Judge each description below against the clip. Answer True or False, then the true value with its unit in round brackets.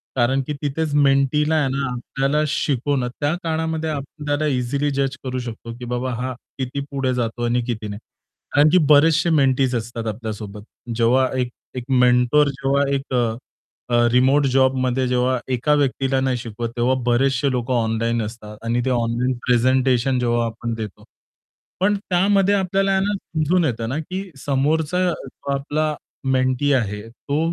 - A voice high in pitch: False (130 Hz)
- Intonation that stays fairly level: False (3.3 semitones)